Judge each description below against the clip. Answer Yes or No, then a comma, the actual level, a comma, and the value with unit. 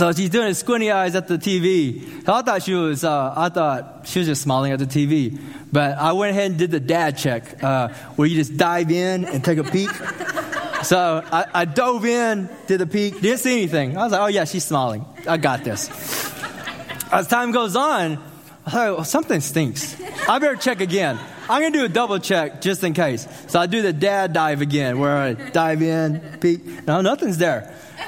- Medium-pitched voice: Yes, medium, 170 Hz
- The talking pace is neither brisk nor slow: No, fast, 215 wpm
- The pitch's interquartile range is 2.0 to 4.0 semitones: No, average, 4.7 semitones